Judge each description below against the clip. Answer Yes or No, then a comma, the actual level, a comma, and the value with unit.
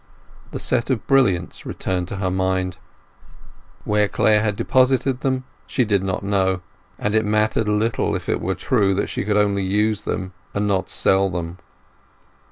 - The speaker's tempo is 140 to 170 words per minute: Yes, average, 165 wpm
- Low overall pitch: Yes, low, 105 Hz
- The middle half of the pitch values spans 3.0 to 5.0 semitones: No, narrow, 2.6 semitones